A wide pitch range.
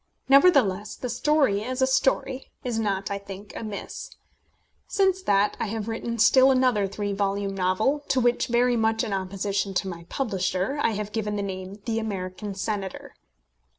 No: average, 4.1 semitones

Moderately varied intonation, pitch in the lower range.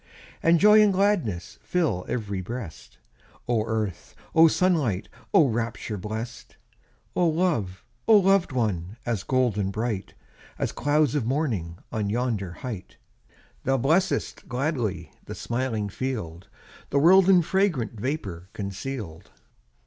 No: wide, 7.5 semitones; low, 120 Hz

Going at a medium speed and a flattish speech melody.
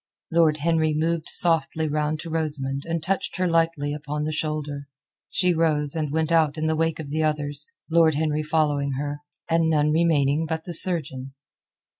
Yes: average, 175 wpm; narrow, 1.8 semitones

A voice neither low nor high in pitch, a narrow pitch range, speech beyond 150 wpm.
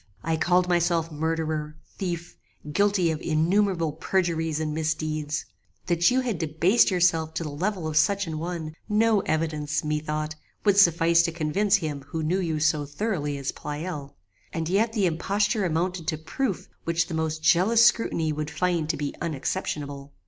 No: medium, 165 Hz; average, 3.0 semitones; average, 165 wpm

